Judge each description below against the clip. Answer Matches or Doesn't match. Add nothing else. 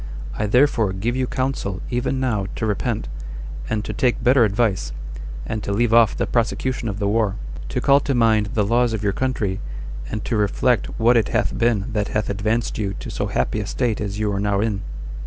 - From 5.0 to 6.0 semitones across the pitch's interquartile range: Doesn't match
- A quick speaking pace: Matches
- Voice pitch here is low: Matches